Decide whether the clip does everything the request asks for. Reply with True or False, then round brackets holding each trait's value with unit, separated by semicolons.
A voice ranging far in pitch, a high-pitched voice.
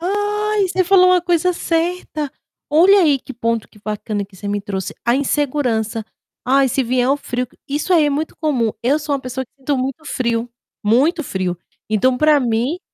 True (6.0 semitones; 275 Hz)